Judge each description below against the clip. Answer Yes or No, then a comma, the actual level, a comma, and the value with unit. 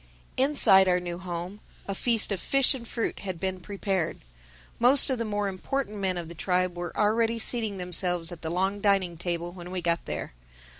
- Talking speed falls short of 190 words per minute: No, average, 195 wpm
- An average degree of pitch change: Yes, average, 3.4 semitones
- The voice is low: No, high, 190 Hz